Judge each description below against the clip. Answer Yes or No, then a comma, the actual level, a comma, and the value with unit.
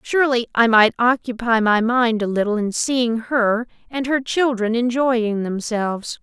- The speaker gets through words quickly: No, average, 155 wpm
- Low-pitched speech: No, high, 235 Hz